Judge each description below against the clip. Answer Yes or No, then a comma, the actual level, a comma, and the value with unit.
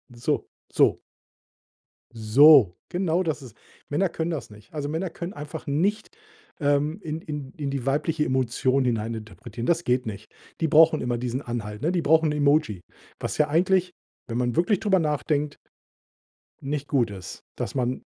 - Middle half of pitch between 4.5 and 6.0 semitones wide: Yes, average, 4.8 semitones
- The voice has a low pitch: No, medium, 145 Hz